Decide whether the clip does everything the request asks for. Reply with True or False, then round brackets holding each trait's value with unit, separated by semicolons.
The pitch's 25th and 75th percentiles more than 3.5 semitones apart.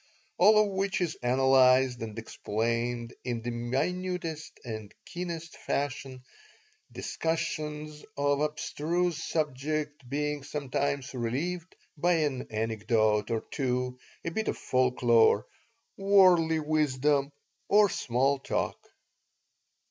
True (4.6 semitones)